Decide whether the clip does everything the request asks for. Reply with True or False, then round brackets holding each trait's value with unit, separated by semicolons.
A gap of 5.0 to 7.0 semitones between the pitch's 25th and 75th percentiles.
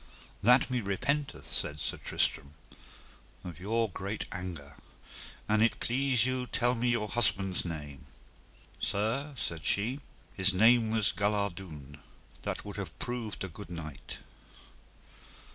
True (5.5 semitones)